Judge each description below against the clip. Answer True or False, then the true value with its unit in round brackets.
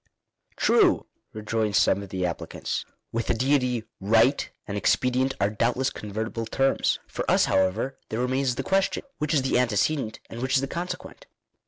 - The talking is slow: False (180 wpm)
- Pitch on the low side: True (120 Hz)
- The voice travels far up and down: False (3.8 semitones)